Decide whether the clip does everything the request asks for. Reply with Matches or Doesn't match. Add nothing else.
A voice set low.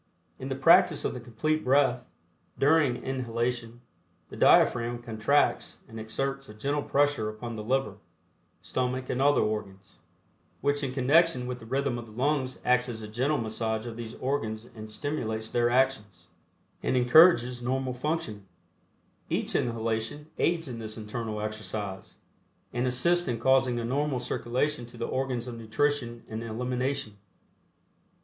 Matches